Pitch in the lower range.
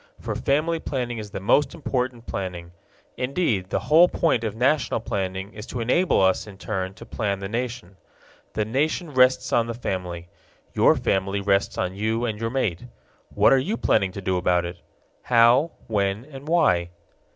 Yes: low, 115 Hz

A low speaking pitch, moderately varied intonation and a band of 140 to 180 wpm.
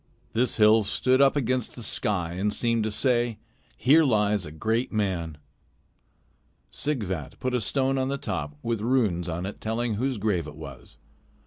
Yes: low, 110 Hz; average, 5.0 semitones; average, 170 wpm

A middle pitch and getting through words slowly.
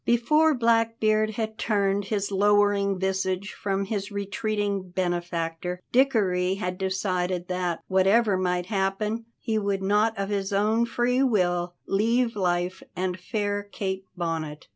No: high, 200 Hz; slow, 130 wpm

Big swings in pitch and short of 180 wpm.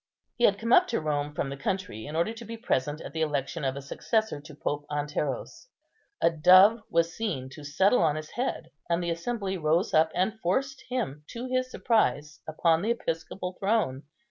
No: wide, 6.9 semitones; average, 195 wpm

